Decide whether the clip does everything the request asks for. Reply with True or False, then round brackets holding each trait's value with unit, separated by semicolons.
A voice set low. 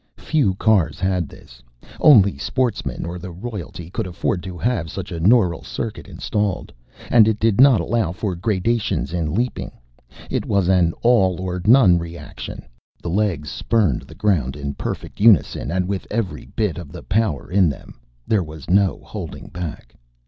True (95 Hz)